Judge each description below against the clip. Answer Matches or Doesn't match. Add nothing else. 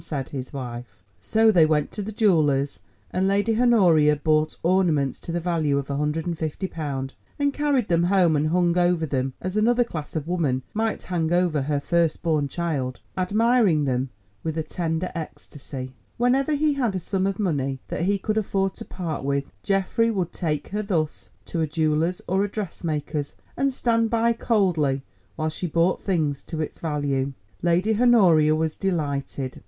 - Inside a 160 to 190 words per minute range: Matches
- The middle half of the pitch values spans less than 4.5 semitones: Doesn't match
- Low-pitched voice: Doesn't match